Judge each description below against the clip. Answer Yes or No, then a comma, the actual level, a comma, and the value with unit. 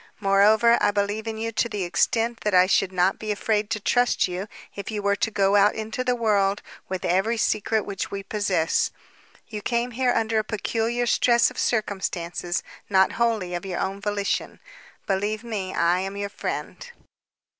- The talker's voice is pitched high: Yes, high, 205 Hz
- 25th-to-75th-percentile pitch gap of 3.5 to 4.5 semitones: No, narrow, 2.5 semitones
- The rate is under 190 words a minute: Yes, average, 180 wpm